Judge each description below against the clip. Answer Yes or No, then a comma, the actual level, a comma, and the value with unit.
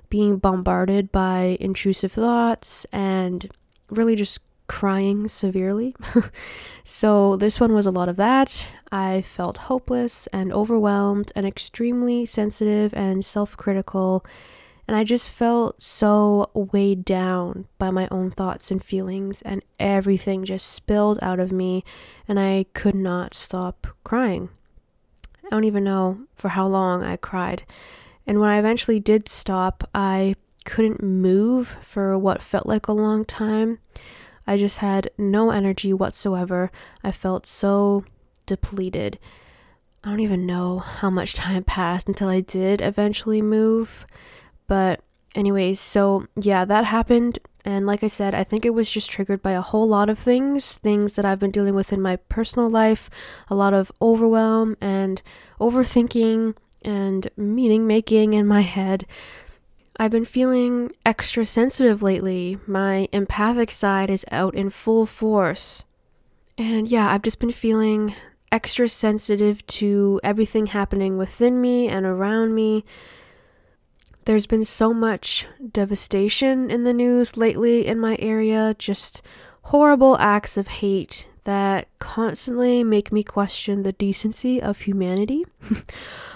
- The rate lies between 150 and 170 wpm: No, average, 140 wpm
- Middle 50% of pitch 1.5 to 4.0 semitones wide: Yes, narrow, 2.4 semitones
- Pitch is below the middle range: No, high, 205 Hz